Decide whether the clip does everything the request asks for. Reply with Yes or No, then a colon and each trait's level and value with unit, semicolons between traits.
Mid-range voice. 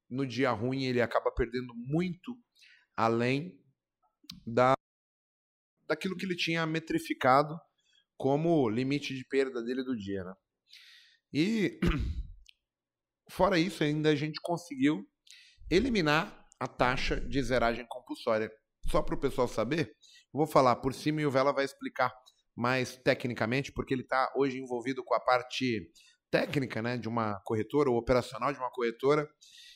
No: low, 130 Hz